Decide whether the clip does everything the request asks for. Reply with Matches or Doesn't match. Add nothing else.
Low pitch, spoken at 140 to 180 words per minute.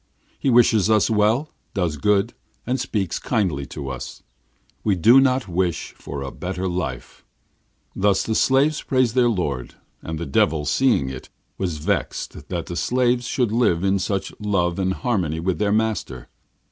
Matches